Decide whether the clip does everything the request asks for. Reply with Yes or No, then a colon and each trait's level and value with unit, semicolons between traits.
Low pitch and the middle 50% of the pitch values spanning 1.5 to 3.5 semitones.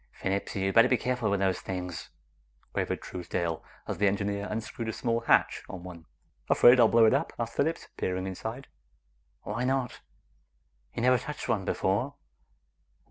No: low, 105 Hz; average, 4.1 semitones